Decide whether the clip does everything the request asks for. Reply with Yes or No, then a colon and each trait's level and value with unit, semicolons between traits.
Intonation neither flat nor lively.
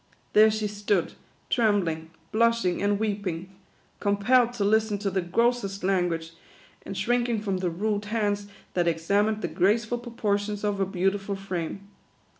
No: narrow, 2.3 semitones